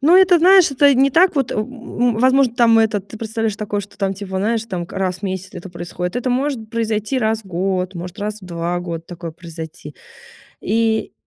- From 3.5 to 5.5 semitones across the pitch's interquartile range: Yes, average, 4.9 semitones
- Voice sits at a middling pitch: No, high, 215 Hz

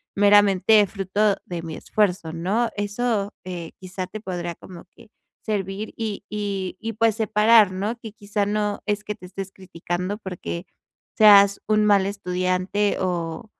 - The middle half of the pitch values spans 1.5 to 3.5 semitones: Yes, narrow, 2.5 semitones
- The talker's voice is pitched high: Yes, high, 200 Hz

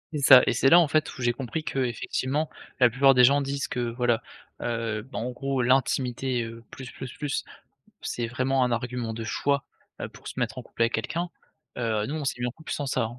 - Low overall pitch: Yes, low, 125 Hz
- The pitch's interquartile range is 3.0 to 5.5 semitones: No, narrow, 2.5 semitones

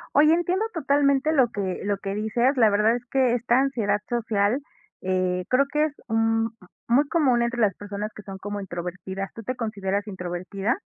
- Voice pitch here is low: No, high, 225 Hz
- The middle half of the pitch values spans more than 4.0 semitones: Yes, average, 4.5 semitones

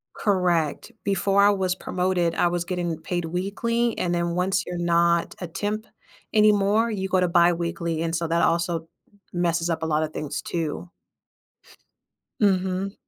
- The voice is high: No, medium, 175 Hz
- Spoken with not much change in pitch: Yes, narrow, 2.3 semitones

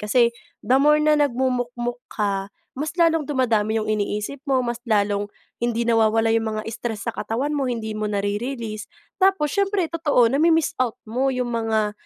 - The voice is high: Yes, high, 235 Hz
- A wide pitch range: No, average, 4.2 semitones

